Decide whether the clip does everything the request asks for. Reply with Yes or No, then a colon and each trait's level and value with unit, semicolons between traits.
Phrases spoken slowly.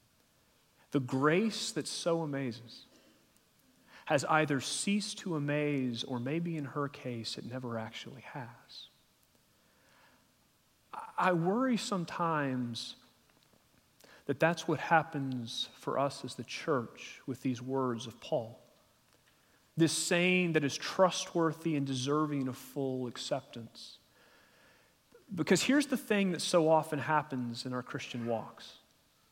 Yes: slow, 120 wpm